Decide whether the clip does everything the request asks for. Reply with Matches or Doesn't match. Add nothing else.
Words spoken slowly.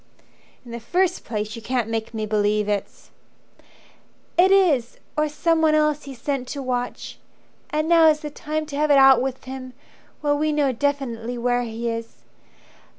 Doesn't match